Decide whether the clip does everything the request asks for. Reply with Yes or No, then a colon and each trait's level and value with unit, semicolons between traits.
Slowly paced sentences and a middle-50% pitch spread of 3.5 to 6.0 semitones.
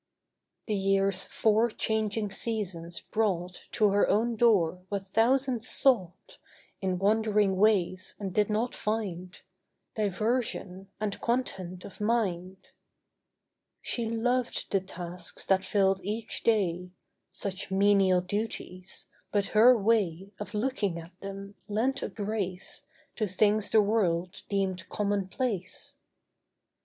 No: slow, 115 wpm; average, 2.9 semitones